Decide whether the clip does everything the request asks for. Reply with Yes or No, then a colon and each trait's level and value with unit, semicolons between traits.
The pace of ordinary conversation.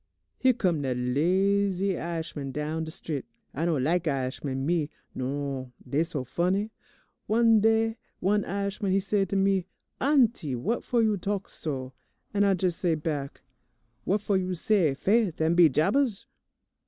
Yes: average, 155 wpm